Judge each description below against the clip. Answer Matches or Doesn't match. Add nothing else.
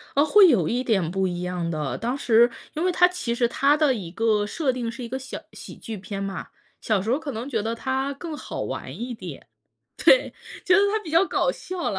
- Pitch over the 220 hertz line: Matches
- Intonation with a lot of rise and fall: Matches